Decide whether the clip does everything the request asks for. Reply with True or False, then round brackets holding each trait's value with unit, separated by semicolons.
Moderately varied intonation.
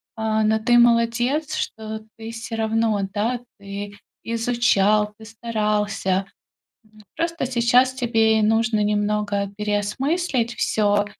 False (2.1 semitones)